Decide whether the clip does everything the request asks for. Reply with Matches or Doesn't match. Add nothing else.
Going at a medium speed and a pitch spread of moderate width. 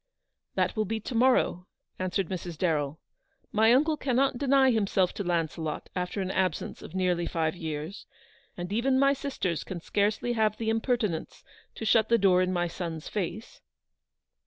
Matches